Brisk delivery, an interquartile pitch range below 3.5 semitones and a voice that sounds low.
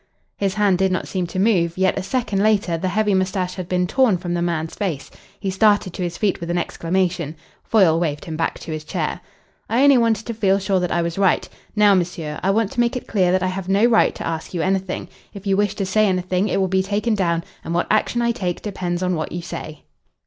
No: fast, 250 wpm; average, 2.9 semitones; medium, 185 Hz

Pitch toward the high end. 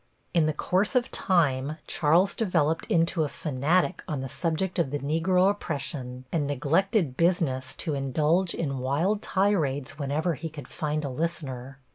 No: medium, 155 Hz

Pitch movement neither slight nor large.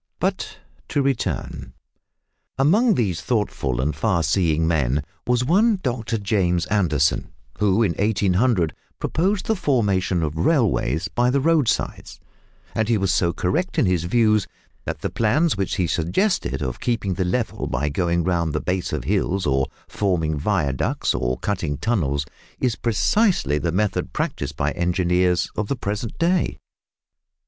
No: wide, 6.5 semitones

